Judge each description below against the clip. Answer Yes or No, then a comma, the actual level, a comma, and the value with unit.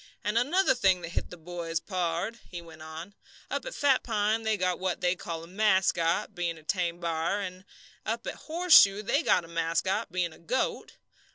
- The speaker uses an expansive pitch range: No, average, 4.2 semitones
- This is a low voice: No, medium, 185 Hz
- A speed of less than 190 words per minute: No, average, 195 wpm